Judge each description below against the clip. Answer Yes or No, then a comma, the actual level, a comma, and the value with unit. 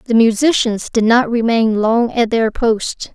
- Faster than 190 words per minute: No, average, 170 wpm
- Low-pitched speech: No, high, 230 Hz